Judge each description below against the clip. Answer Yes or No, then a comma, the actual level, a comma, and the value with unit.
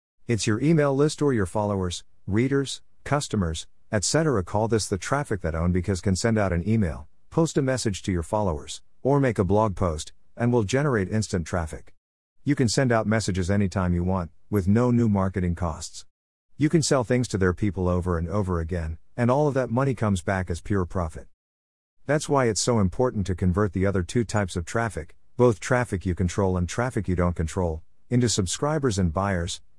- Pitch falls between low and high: No, low, 100 Hz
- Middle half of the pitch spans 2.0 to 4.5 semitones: No, average, 5.1 semitones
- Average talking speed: Yes, average, 195 wpm